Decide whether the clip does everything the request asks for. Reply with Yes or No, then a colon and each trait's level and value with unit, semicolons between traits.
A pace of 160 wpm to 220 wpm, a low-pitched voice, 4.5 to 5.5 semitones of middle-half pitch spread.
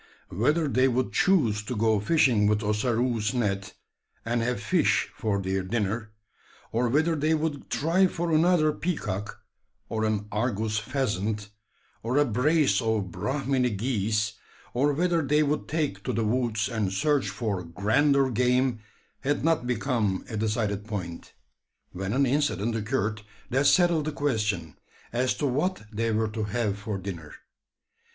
No: average, 150 wpm; low, 115 Hz; average, 5.2 semitones